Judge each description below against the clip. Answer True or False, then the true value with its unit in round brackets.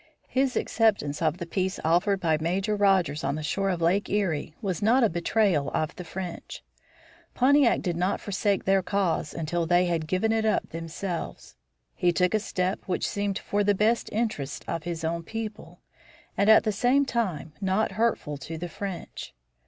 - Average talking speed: True (180 wpm)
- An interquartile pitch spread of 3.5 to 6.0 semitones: True (3.9 semitones)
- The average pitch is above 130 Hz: True (190 Hz)